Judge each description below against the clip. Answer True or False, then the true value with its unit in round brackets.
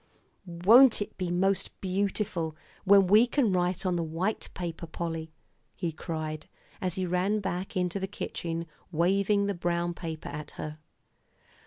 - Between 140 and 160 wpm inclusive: True (150 wpm)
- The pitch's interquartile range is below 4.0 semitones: True (2.8 semitones)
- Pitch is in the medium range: True (180 Hz)